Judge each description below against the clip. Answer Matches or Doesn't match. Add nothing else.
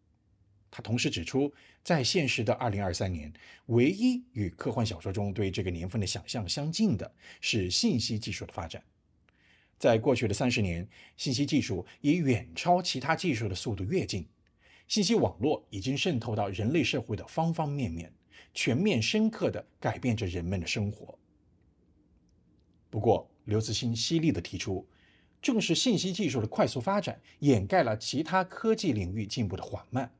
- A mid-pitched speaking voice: Doesn't match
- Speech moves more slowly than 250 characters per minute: Doesn't match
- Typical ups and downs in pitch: Doesn't match